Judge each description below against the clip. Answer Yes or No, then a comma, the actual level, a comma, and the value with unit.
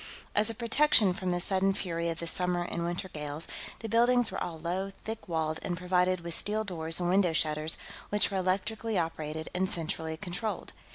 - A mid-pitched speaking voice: Yes, medium, 180 Hz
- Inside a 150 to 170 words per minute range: No, average, 190 wpm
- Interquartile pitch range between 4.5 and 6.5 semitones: No, average, 3.4 semitones